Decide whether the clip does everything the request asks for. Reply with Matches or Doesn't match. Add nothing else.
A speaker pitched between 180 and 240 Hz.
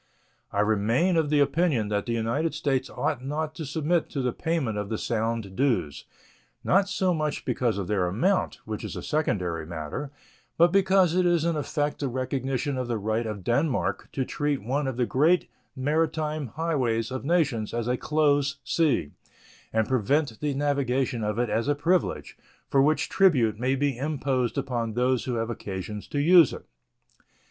Doesn't match